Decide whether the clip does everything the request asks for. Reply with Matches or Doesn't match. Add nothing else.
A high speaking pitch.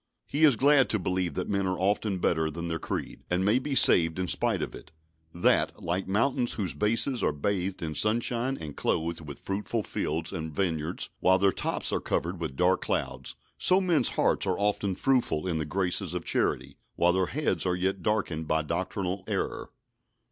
Doesn't match